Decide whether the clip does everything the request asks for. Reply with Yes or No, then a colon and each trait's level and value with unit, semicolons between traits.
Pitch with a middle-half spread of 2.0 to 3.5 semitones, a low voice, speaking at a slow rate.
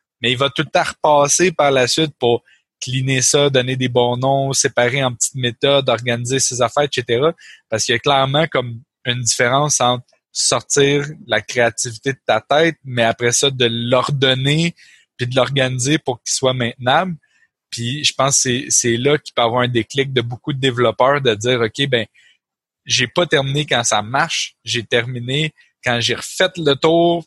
No: average, 2.9 semitones; low, 130 Hz; average, 185 wpm